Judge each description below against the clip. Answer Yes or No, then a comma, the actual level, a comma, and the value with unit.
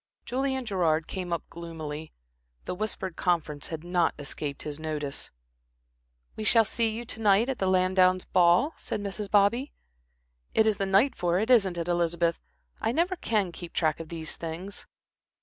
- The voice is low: No, medium, 185 Hz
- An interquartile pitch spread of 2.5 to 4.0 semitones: No, average, 4.6 semitones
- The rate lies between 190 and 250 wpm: No, average, 165 wpm